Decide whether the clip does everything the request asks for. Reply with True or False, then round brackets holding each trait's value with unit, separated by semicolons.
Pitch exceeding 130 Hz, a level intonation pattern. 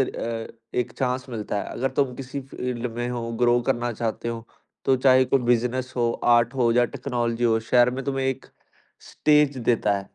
False (120 Hz; 1.8 semitones)